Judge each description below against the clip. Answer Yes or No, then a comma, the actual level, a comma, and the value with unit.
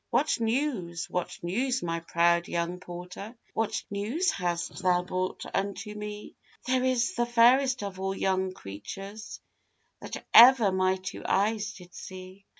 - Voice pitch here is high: Yes, high, 195 Hz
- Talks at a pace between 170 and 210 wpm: No, average, 145 wpm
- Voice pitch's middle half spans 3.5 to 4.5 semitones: Yes, average, 4.0 semitones